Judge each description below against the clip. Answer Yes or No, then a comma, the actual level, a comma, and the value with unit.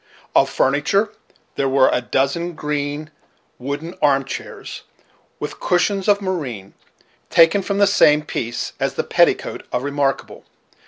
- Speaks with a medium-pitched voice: Yes, medium, 150 Hz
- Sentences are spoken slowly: Yes, slow, 130 wpm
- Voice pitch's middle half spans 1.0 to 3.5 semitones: No, average, 4.7 semitones